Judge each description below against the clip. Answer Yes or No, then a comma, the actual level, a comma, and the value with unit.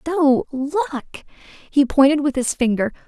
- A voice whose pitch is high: Yes, very high, 280 Hz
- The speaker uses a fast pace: No, slow, 135 wpm